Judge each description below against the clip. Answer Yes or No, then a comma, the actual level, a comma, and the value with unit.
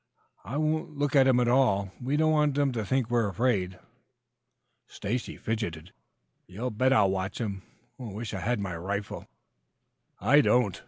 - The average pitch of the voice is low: Yes, low, 115 Hz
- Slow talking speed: No, average, 160 wpm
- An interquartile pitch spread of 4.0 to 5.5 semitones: Yes, average, 5.0 semitones